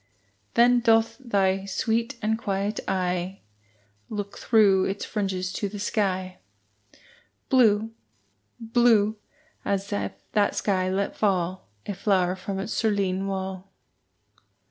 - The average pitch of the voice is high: Yes, high, 200 Hz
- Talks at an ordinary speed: No, slow, 115 wpm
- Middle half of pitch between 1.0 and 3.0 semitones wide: Yes, narrow, 2.6 semitones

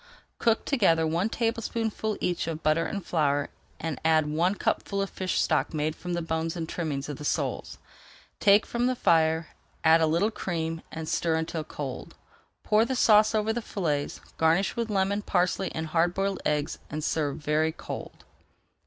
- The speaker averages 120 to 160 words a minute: No, average, 175 wpm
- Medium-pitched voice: Yes, medium, 165 Hz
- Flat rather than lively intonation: No, average, 4.2 semitones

